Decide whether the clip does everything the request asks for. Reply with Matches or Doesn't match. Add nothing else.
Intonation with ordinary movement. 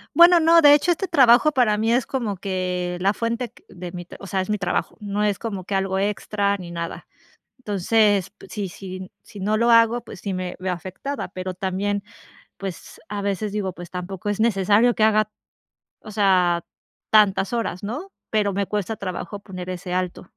Matches